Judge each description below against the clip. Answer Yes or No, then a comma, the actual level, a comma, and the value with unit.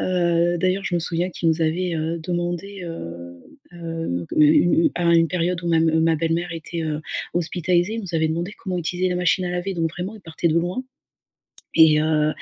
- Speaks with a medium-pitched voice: Yes, medium, 170 Hz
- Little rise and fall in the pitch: Yes, narrow, 1.7 semitones